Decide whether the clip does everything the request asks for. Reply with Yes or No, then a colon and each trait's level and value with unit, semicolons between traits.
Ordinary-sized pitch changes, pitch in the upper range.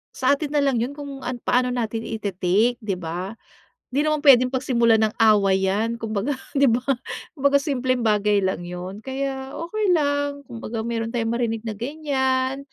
Yes: average, 4.2 semitones; high, 245 Hz